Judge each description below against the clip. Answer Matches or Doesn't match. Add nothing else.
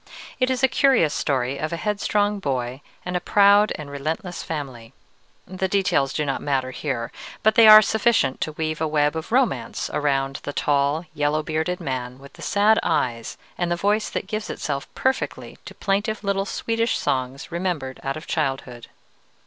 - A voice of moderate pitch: Matches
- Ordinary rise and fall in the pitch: Doesn't match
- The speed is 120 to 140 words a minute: Doesn't match